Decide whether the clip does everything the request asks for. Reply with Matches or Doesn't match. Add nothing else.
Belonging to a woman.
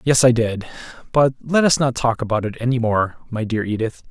Doesn't match